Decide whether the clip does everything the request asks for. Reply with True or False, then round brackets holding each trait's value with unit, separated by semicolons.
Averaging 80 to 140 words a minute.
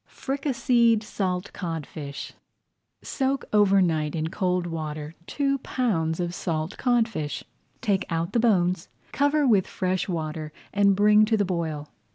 True (135 wpm)